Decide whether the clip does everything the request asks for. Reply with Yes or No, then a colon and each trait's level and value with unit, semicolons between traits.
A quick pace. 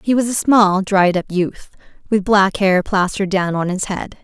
Yes: fast, 215 wpm